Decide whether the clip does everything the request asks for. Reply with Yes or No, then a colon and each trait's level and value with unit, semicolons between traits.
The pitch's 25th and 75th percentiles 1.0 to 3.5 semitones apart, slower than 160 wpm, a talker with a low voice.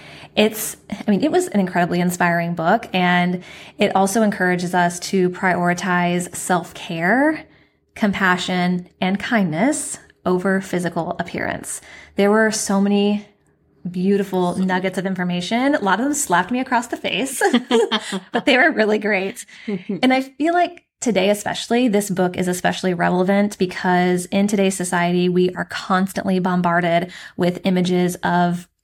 No: average, 3.1 semitones; average, 140 wpm; high, 190 Hz